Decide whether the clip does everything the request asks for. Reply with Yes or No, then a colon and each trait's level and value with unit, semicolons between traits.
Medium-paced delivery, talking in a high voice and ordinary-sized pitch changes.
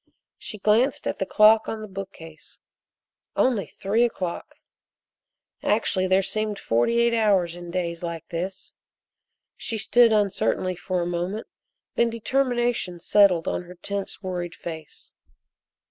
No: slow, 130 wpm; high, 195 Hz; average, 3.8 semitones